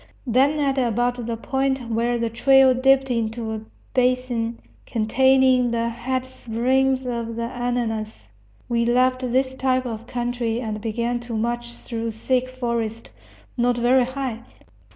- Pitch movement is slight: Yes, narrow, 1.8 semitones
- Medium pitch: No, high, 245 Hz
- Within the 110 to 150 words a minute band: Yes, average, 140 wpm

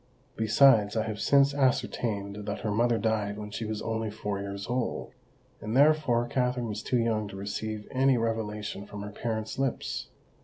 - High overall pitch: No, low, 110 Hz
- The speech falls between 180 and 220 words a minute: No, average, 170 wpm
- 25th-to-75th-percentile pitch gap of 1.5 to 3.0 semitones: Yes, average, 2.7 semitones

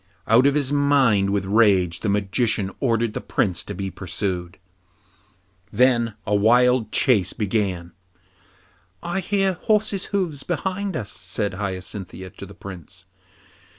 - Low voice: Yes, low, 105 Hz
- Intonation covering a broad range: Yes, wide, 6.1 semitones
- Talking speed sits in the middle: No, slow, 130 wpm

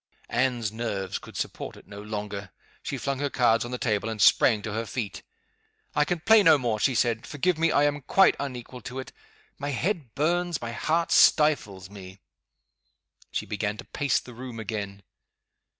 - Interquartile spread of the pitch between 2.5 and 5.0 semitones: No, wide, 5.4 semitones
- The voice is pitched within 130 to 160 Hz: No, low, 120 Hz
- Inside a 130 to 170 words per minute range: No, average, 180 wpm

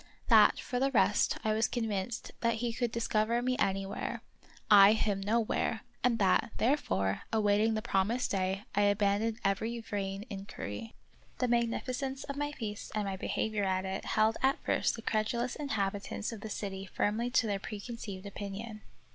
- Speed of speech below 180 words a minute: Yes, average, 165 wpm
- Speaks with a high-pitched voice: Yes, high, 215 Hz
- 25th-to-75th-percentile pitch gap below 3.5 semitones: Yes, average, 2.9 semitones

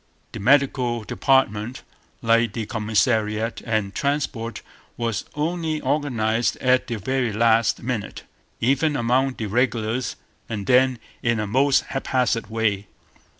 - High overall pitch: No, low, 120 Hz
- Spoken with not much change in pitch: No, average, 3.2 semitones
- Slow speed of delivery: Yes, slow, 120 wpm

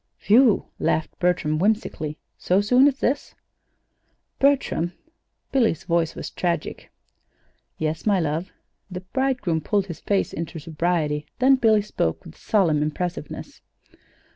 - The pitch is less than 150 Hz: No, medium, 180 Hz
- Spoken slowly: Yes, slow, 120 wpm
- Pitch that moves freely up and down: Yes, wide, 5.7 semitones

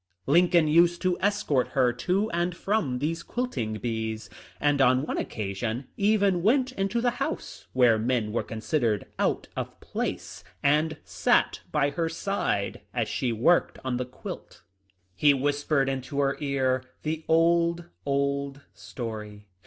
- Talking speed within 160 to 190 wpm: No, average, 150 wpm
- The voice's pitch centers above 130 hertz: Yes, medium, 140 Hz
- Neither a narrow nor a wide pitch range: No, wide, 5.8 semitones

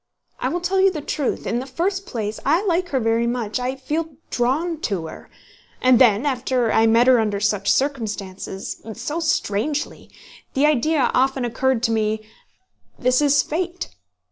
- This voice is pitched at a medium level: No, very high, 255 Hz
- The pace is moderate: Yes, average, 165 wpm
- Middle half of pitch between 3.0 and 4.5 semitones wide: No, average, 5.1 semitones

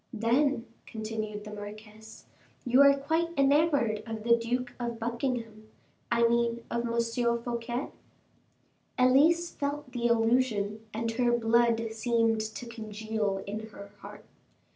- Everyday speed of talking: No, slow, 125 wpm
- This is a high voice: Yes, high, 235 Hz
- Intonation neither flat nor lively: No, narrow, 2.2 semitones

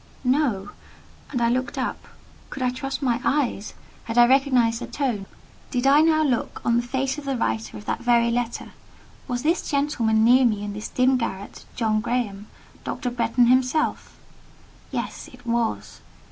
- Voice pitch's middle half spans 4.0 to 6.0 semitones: No, average, 2.7 semitones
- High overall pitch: Yes, high, 245 Hz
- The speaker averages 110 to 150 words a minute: No, average, 165 wpm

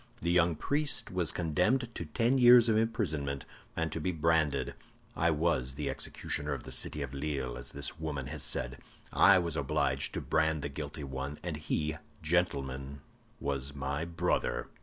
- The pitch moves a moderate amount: Yes, average, 3.7 semitones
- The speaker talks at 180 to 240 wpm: No, average, 165 wpm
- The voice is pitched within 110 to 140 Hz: No, very low, 75 Hz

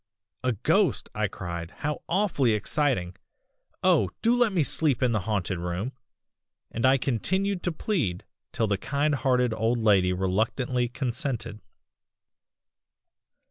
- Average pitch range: No, wide, 6.2 semitones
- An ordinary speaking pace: No, slow, 130 wpm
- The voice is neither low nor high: No, low, 120 Hz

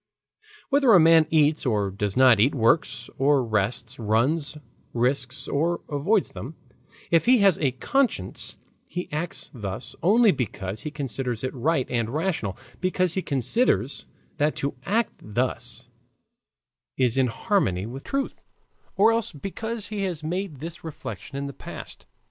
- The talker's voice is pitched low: No, medium, 145 Hz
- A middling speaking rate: Yes, average, 150 wpm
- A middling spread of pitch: No, wide, 6.5 semitones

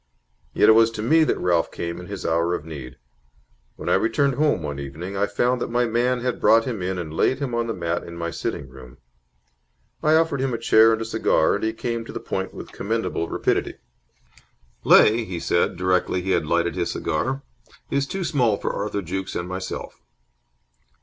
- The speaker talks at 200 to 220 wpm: Yes, fast, 205 wpm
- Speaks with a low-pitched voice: Yes, low, 100 Hz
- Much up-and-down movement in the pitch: Yes, wide, 5.7 semitones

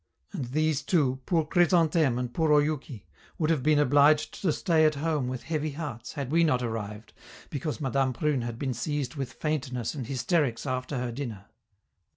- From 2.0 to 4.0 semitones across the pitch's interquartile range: Yes, average, 3.7 semitones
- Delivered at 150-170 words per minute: No, average, 180 wpm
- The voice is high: No, medium, 140 Hz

